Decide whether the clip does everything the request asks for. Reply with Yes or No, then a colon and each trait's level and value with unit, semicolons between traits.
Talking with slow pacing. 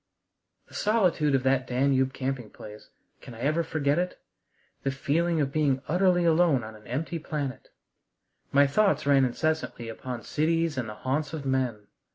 No: average, 165 wpm